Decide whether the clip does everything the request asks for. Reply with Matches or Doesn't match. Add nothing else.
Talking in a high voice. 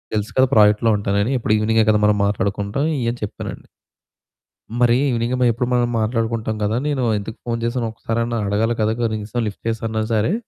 Doesn't match